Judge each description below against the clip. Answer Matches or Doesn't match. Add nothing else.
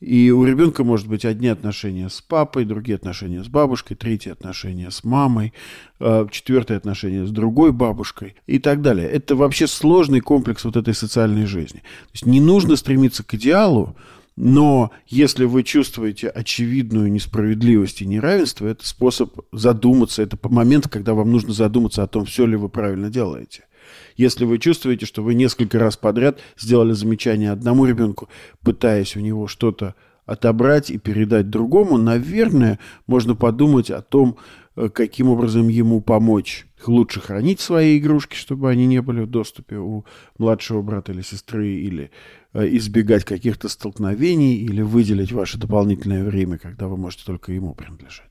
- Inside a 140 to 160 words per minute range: Matches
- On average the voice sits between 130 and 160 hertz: Doesn't match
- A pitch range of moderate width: Matches